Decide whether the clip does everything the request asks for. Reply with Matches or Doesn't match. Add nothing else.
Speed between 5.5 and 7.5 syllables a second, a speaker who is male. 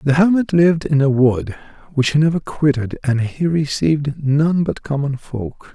Doesn't match